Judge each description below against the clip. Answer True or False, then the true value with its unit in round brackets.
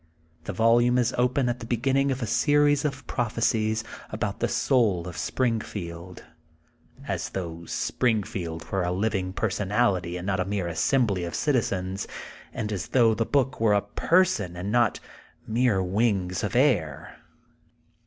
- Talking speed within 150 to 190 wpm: True (155 wpm)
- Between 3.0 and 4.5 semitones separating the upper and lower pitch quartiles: False (5.0 semitones)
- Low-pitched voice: True (110 Hz)